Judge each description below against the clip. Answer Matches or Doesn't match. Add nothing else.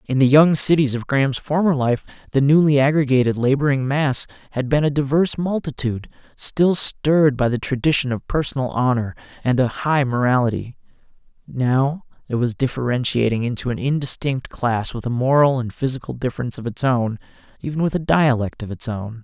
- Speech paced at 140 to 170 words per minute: Matches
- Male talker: Matches